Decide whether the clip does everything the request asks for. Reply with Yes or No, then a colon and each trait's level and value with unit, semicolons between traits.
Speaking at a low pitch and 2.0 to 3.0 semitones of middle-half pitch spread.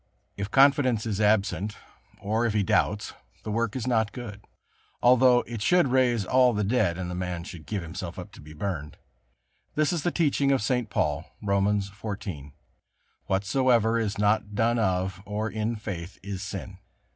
No: low, 105 Hz; average, 3.5 semitones